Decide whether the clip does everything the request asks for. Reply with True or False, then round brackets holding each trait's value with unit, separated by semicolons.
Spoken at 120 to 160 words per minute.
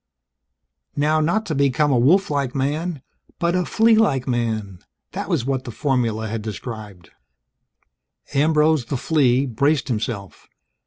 True (140 wpm)